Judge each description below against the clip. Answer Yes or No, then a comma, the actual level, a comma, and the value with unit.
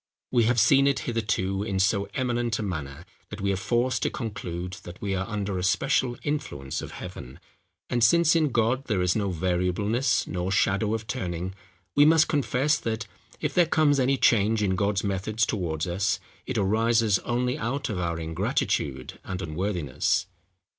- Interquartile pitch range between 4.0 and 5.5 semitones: Yes, average, 4.7 semitones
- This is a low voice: Yes, low, 105 Hz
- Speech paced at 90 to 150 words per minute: No, average, 175 wpm